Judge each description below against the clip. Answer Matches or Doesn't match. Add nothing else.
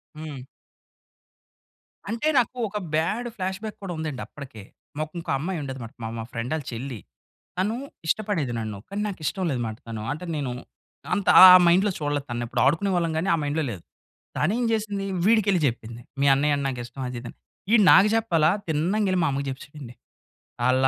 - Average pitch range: Doesn't match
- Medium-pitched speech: Matches